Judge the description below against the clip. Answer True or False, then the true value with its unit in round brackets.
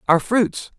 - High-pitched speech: True (200 Hz)